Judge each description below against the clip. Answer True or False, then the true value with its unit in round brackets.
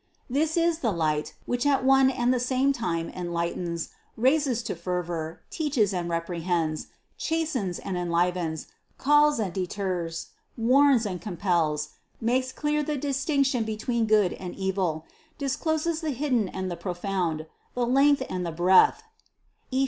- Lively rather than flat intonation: True (7.6 semitones)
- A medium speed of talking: True (150 wpm)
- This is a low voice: False (215 Hz)